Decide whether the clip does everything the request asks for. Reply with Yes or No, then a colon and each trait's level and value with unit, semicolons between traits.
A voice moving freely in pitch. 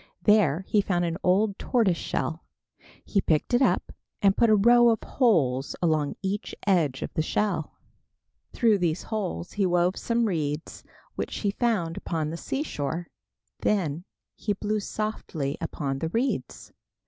No: average, 5.0 semitones